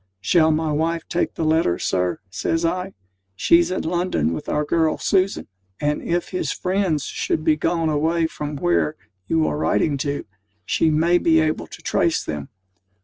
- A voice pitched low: No, medium, 160 Hz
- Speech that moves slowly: No, average, 170 wpm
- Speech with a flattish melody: Yes, narrow, 2.3 semitones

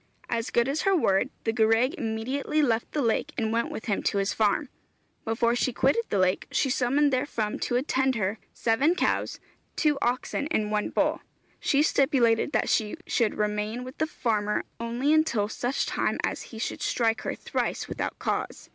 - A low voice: No, high, 235 Hz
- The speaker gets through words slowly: No, average, 180 wpm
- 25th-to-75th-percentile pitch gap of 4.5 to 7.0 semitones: No, average, 3.9 semitones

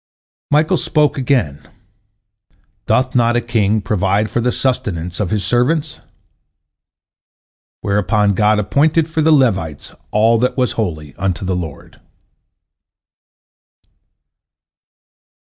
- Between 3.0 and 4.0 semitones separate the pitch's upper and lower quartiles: No, average, 5.0 semitones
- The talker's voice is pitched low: Yes, low, 110 Hz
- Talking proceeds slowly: Yes, slow, 105 wpm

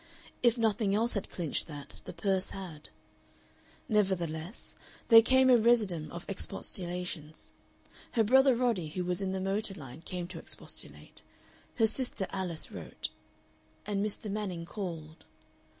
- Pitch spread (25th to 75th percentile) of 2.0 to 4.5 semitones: Yes, average, 4.1 semitones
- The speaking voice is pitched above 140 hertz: Yes, high, 190 Hz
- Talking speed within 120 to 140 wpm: Yes, slow, 135 wpm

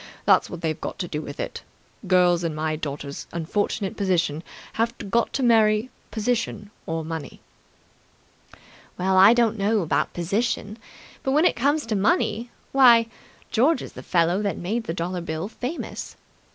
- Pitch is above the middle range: Yes, high, 200 Hz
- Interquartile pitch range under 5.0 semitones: No, wide, 5.6 semitones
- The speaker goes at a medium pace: Yes, average, 160 wpm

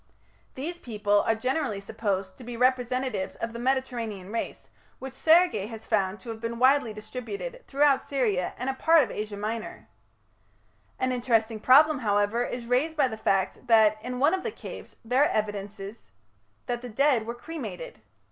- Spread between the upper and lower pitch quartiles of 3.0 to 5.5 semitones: Yes, average, 3.8 semitones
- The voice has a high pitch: Yes, high, 240 Hz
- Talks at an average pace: Yes, average, 170 wpm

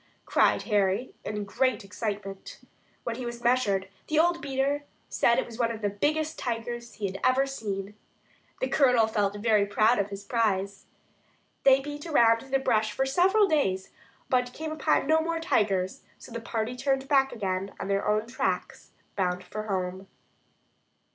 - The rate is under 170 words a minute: No, average, 175 wpm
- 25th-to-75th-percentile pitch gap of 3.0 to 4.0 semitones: No, average, 5.0 semitones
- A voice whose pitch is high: Yes, high, 230 Hz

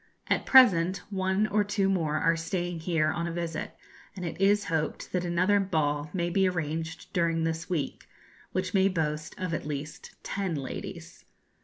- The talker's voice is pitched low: No, medium, 170 Hz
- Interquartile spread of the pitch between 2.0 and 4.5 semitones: Yes, average, 2.8 semitones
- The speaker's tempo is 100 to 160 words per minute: No, average, 170 wpm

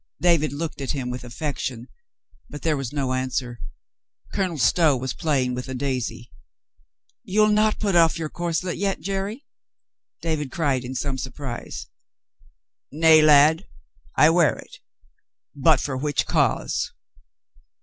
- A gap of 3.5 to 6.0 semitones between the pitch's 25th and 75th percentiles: Yes, average, 4.3 semitones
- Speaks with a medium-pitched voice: Yes, medium, 150 Hz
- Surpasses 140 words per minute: No, slow, 135 wpm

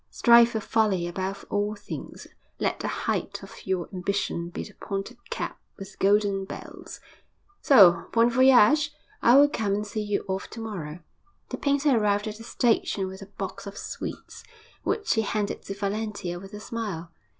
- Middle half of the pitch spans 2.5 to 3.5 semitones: Yes, average, 2.8 semitones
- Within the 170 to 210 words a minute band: Yes, average, 175 wpm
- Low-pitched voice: No, high, 205 Hz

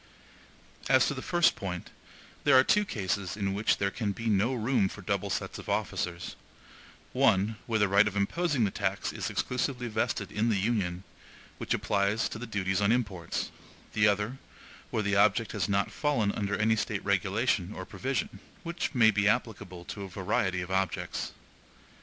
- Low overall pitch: Yes, low, 105 Hz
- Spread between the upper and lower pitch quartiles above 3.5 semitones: No, average, 3.1 semitones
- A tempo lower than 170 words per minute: No, average, 175 wpm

